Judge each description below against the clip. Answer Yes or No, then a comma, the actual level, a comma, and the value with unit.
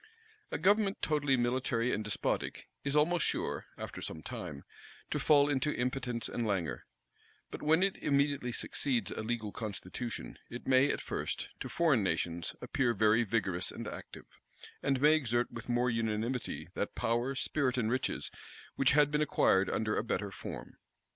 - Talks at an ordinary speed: Yes, average, 160 wpm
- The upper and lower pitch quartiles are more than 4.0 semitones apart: Yes, average, 4.4 semitones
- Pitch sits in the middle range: No, low, 125 Hz